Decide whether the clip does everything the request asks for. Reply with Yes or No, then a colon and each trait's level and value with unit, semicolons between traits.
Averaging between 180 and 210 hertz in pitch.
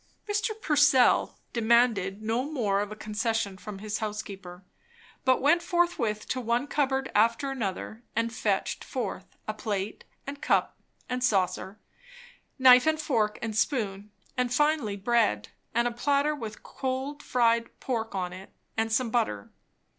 No: high, 230 Hz